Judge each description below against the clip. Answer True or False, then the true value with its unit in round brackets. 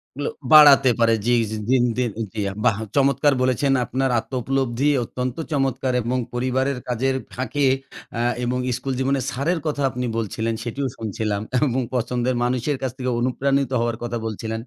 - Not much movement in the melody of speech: True (2.3 semitones)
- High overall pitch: False (130 Hz)